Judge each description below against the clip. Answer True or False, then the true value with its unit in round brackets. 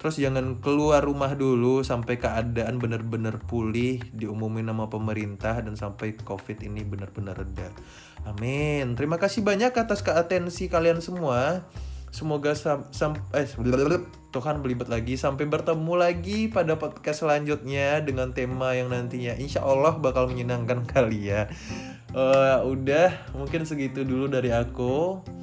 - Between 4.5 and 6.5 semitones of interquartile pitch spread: True (4.8 semitones)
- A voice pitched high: False (130 Hz)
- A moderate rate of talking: True (130 wpm)